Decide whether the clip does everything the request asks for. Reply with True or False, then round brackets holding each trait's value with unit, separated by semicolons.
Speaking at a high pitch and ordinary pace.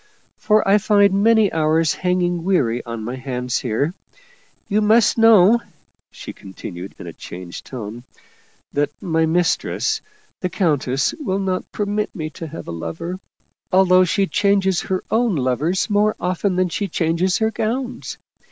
False (180 Hz; 155 wpm)